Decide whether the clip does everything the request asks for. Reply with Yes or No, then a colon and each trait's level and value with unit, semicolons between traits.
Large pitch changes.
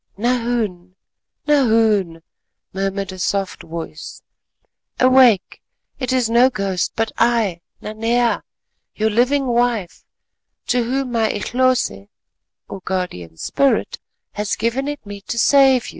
No: average, 4.3 semitones